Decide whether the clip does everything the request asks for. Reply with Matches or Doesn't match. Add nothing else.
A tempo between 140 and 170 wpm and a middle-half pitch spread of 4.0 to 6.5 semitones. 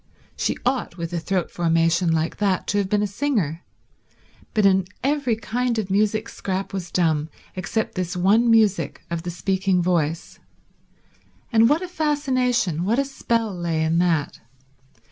Matches